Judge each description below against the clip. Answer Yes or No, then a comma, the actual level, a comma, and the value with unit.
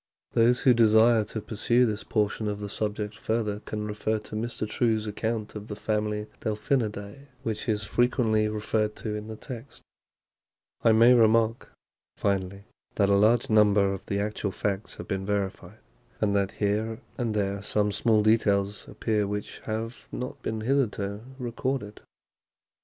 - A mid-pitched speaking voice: No, low, 105 Hz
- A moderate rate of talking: Yes, average, 155 wpm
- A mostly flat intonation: Yes, narrow, 1.6 semitones